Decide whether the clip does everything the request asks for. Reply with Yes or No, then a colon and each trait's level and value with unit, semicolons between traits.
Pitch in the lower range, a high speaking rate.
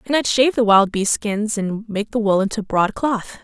No: high, 215 Hz; fast, 245 wpm